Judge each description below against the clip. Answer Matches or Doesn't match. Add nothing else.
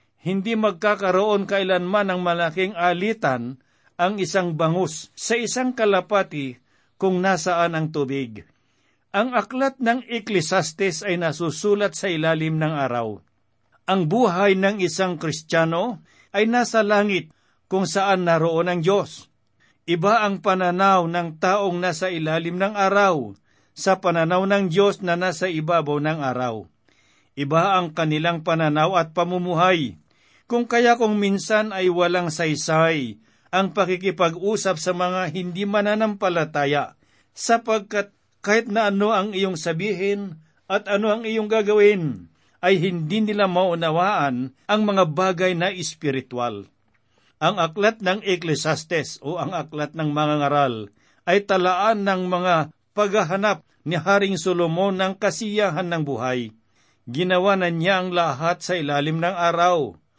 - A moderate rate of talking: Matches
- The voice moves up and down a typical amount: Matches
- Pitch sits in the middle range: Matches